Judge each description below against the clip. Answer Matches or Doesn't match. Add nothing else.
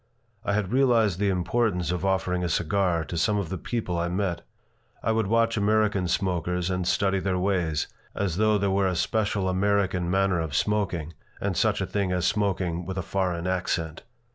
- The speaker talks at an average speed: Matches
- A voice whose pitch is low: Matches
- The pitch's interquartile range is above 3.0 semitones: Doesn't match